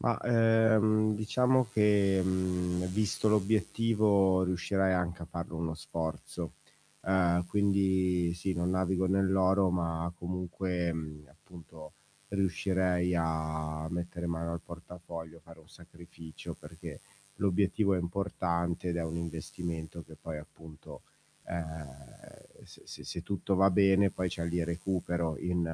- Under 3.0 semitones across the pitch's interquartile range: Yes, narrow, 2.5 semitones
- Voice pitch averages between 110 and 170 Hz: No, very low, 90 Hz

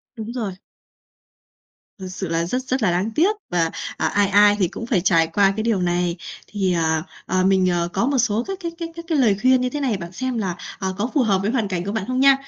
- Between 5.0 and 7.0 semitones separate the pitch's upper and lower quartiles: Yes, wide, 5.6 semitones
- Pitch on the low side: No, high, 205 Hz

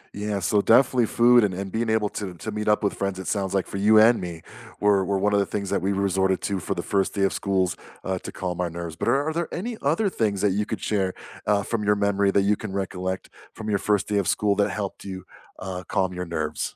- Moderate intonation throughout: No, narrow, 2.0 semitones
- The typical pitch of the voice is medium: No, low, 100 Hz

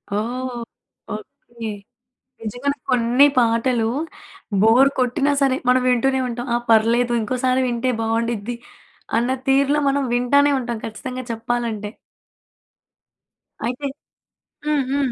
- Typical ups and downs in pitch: No, narrow, 2.2 semitones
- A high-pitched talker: Yes, high, 245 Hz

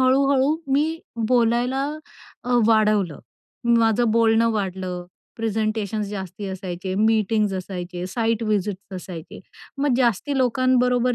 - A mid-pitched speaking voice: No, high, 220 Hz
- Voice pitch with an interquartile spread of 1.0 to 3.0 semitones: No, average, 4.3 semitones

